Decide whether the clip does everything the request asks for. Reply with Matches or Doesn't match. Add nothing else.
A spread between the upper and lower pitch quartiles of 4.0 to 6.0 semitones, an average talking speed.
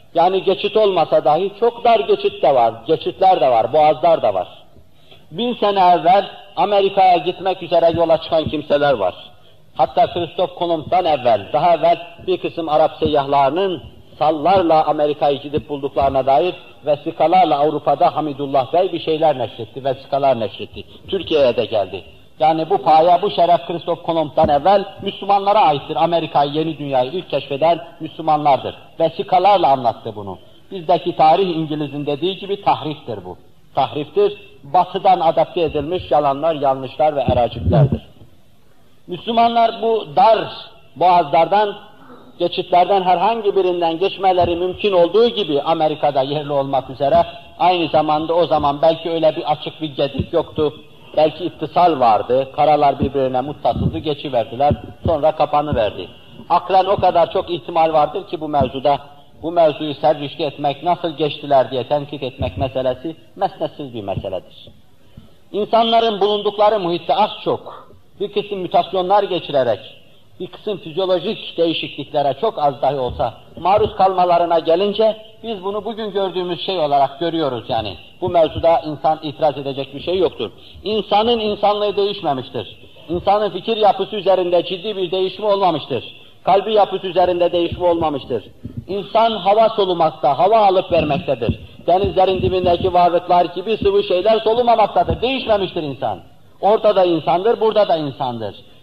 Matches